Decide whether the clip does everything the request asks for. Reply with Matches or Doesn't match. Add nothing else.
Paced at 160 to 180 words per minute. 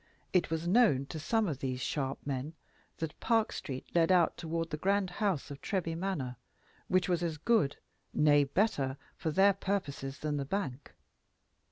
Matches